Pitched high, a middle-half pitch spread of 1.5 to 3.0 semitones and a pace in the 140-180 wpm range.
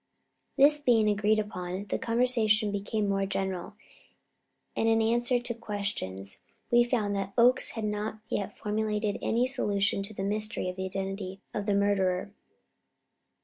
Yes: high, 210 Hz; narrow, 2.4 semitones; average, 150 wpm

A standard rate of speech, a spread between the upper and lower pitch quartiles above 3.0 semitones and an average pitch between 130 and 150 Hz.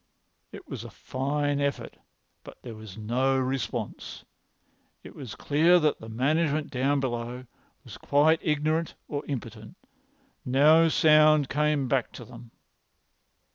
No: slow, 130 wpm; average, 3.4 semitones; medium, 140 Hz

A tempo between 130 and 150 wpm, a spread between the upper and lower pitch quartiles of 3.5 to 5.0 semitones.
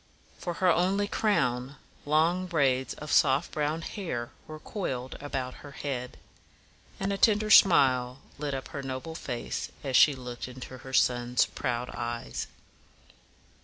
Yes: average, 140 wpm; average, 4.7 semitones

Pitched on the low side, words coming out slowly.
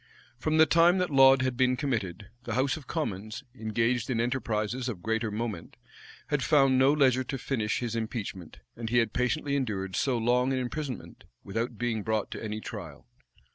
No: low, 120 Hz; average, 180 wpm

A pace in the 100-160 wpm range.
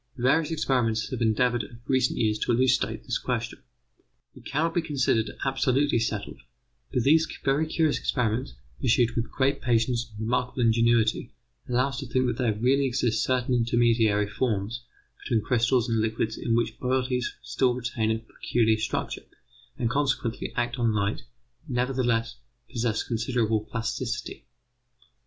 Yes: average, 145 wpm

